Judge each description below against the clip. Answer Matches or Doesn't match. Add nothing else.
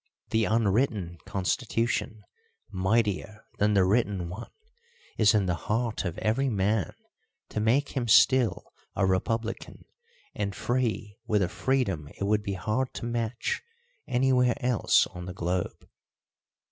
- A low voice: Matches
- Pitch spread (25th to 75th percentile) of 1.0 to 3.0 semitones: Doesn't match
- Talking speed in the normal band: Doesn't match